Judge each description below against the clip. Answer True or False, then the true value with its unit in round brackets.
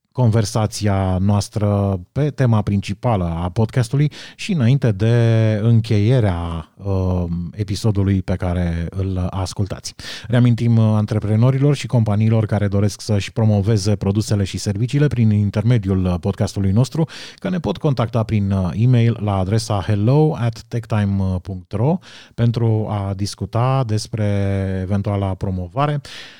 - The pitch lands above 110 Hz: False (105 Hz)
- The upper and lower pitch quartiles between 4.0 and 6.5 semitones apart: False (3.1 semitones)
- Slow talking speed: True (110 wpm)